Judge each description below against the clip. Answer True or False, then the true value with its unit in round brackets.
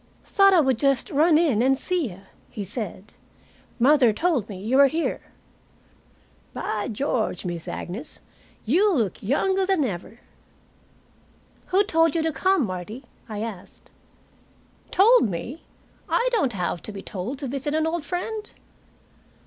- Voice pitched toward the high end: True (270 Hz)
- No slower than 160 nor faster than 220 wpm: False (145 wpm)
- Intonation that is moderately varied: False (7.9 semitones)